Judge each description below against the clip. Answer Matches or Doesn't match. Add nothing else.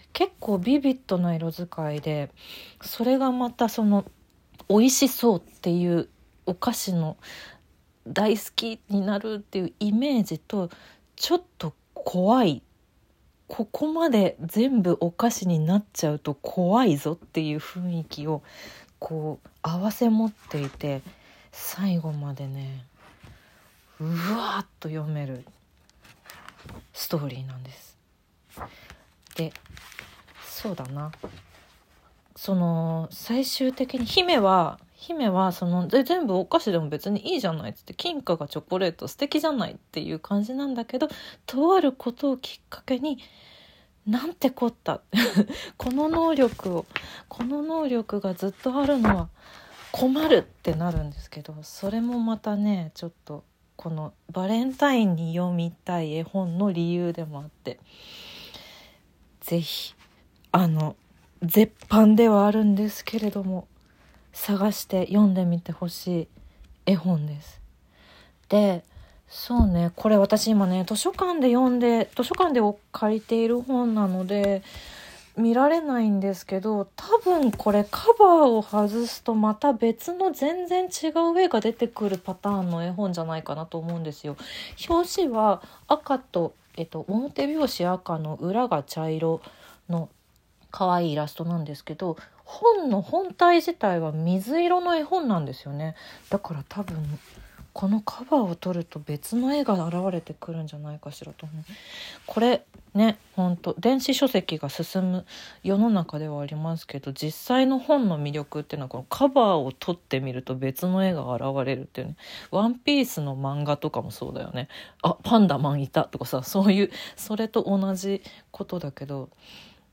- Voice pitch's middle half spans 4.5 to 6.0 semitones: Doesn't match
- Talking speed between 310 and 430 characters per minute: Doesn't match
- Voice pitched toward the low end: Doesn't match